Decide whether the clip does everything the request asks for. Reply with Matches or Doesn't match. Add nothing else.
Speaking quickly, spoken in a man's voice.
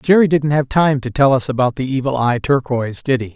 Matches